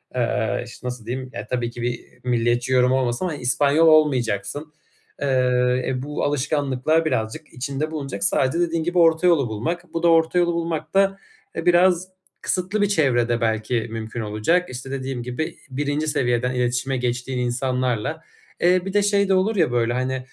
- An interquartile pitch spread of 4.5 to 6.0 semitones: Yes, average, 4.9 semitones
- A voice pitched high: No, low, 130 Hz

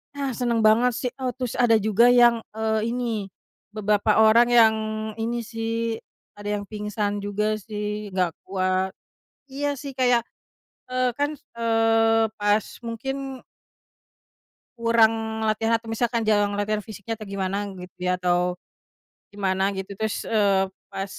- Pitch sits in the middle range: No, high, 220 Hz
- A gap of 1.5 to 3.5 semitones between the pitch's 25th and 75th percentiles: Yes, narrow, 2.4 semitones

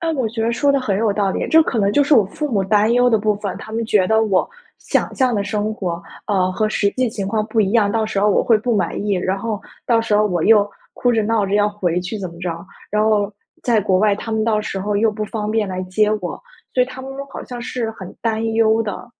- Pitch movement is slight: Yes, narrow, 2.0 semitones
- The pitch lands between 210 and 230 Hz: Yes, high, 215 Hz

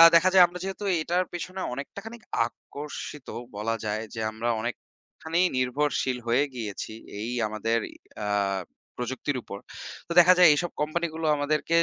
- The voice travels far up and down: Yes, wide, 6.6 semitones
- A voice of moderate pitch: Yes, medium, 145 Hz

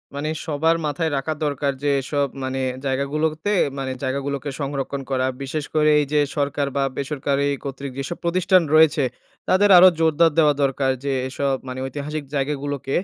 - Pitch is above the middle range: No, medium, 145 Hz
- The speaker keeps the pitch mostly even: Yes, narrow, 2.1 semitones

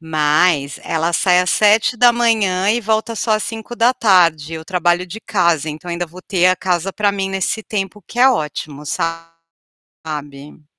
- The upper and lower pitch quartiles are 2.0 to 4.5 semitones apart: No, average, 5.0 semitones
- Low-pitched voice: No, medium, 185 Hz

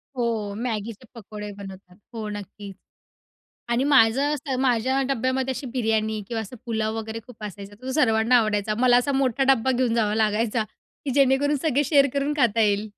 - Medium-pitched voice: No, high, 230 Hz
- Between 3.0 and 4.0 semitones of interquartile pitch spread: Yes, average, 3.5 semitones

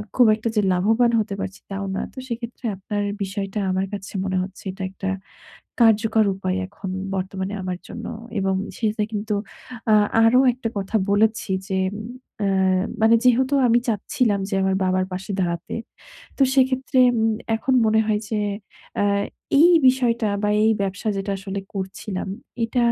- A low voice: No, high, 205 Hz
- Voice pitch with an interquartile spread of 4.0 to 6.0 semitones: No, average, 3.0 semitones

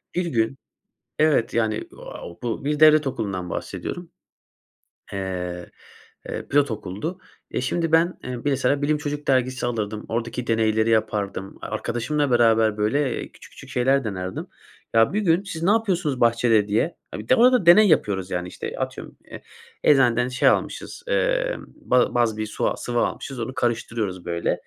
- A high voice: No, low, 120 Hz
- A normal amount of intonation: No, wide, 5.7 semitones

